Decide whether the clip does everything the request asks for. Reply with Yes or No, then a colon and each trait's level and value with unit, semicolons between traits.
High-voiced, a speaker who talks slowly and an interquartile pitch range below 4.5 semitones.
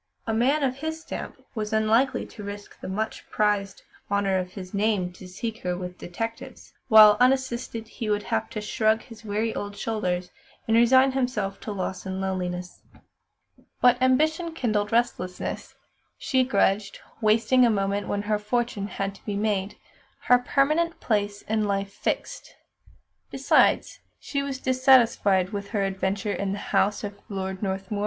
No: high, 210 Hz; average, 160 wpm; average, 3.4 semitones